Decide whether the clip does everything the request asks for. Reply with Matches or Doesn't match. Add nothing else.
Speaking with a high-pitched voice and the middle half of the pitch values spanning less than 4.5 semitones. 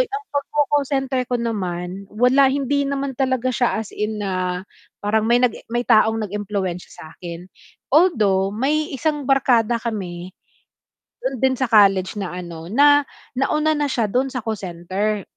Doesn't match